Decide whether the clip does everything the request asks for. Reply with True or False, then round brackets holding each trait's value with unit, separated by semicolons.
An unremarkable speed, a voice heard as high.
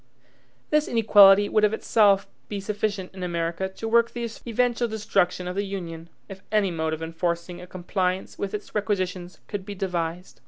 True (170 wpm; 195 Hz)